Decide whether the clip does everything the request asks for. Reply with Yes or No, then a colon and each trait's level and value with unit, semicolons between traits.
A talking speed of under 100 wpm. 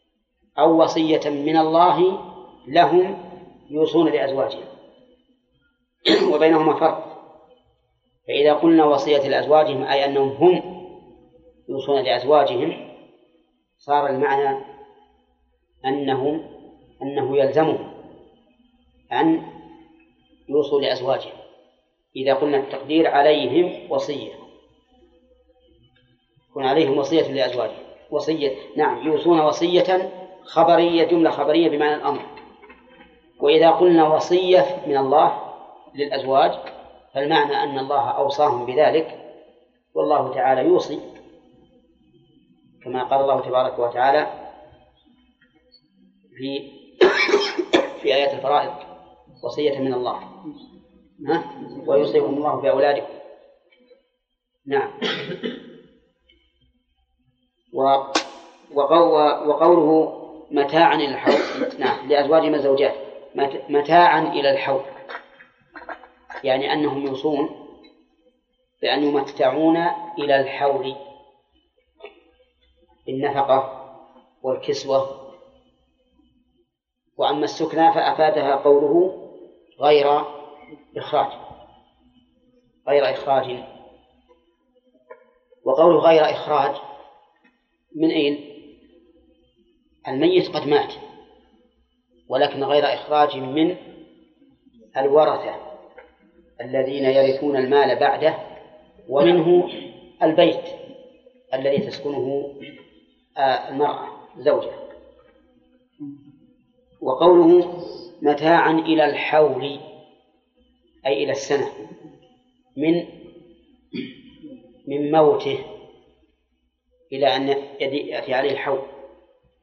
Yes: average, 70 wpm